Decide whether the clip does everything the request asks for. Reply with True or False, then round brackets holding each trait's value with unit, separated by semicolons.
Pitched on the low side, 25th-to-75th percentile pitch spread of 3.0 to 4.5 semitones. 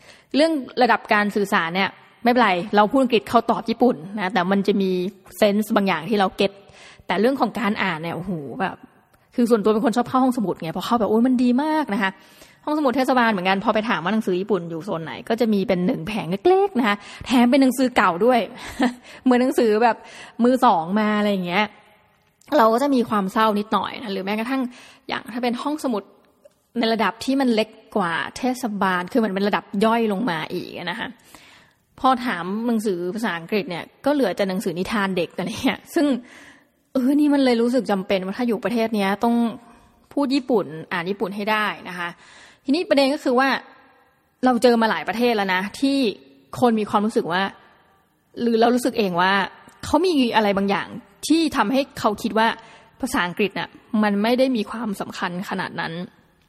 False (220 Hz; 4.0 semitones)